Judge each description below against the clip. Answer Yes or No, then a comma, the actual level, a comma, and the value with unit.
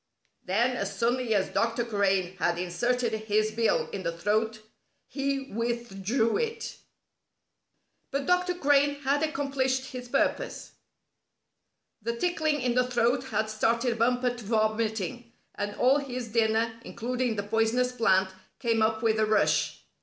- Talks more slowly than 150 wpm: Yes, average, 140 wpm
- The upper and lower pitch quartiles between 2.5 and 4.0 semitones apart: Yes, average, 2.8 semitones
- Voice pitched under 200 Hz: No, high, 235 Hz